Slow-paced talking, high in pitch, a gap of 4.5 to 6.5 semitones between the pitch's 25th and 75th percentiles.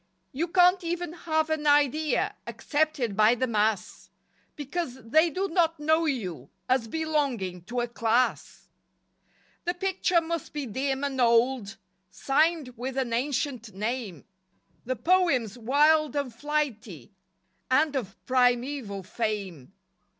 Yes: slow, 125 wpm; very high, 265 Hz; average, 5.3 semitones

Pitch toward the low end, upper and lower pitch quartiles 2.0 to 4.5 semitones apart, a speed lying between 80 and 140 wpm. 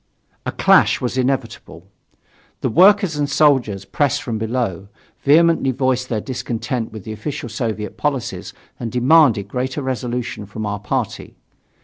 Yes: low, 125 Hz; average, 4.1 semitones; slow, 135 wpm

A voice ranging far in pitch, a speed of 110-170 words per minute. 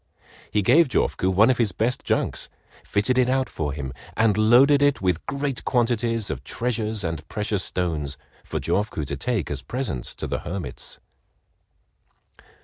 Yes: wide, 6.3 semitones; average, 155 wpm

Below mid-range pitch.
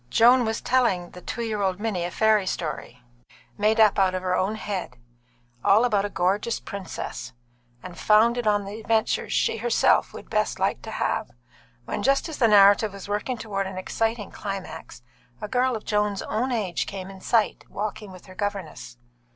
No: high, 205 Hz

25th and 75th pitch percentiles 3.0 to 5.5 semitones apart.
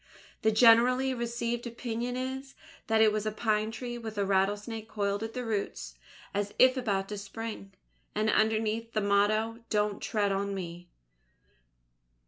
No: narrow, 2.4 semitones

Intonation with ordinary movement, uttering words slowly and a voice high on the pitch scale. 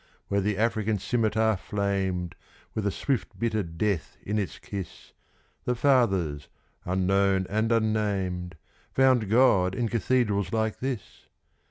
No: average, 3.2 semitones; slow, 125 wpm; low, 105 Hz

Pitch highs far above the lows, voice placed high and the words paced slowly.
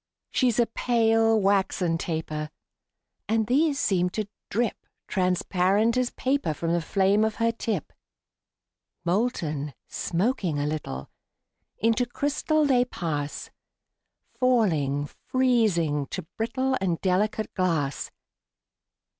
Yes: wide, 6.1 semitones; high, 200 Hz; slow, 105 wpm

